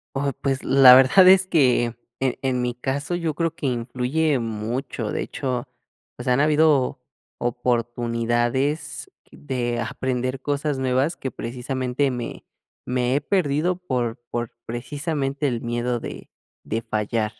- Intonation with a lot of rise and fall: No, average, 3.0 semitones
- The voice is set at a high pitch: No, low, 130 Hz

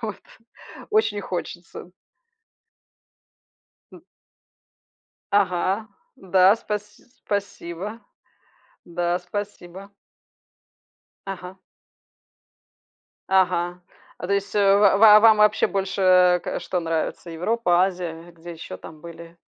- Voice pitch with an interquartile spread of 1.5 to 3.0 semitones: Yes, average, 2.7 semitones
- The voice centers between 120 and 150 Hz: No, medium, 185 Hz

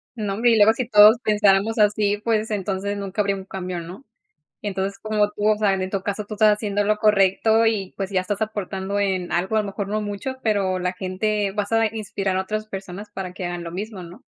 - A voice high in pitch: Yes, high, 205 Hz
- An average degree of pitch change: No, narrow, 2.0 semitones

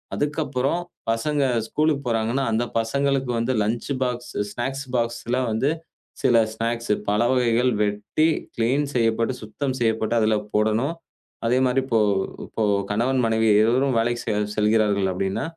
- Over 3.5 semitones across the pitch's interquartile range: No, average, 2.9 semitones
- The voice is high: No, low, 120 Hz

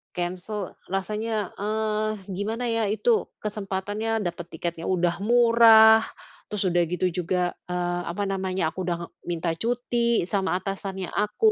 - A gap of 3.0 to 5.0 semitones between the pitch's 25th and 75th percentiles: Yes, average, 3.6 semitones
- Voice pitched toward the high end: Yes, high, 200 Hz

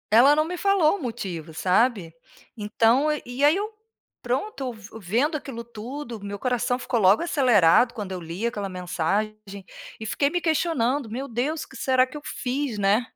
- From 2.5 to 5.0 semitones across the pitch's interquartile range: No, wide, 5.5 semitones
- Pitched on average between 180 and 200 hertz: No, high, 240 Hz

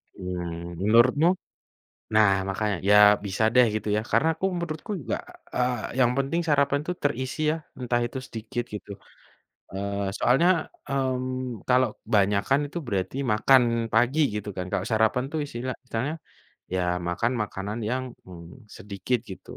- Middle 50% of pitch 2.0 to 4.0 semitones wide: No, average, 4.6 semitones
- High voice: No, low, 120 Hz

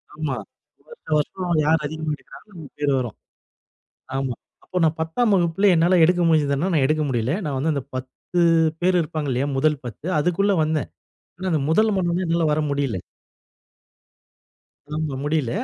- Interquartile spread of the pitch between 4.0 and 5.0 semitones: No, average, 3.6 semitones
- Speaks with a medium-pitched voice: Yes, medium, 155 Hz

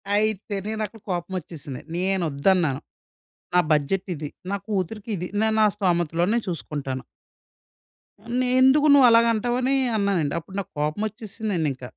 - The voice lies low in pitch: No, high, 190 Hz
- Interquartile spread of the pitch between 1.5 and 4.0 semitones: No, average, 5.2 semitones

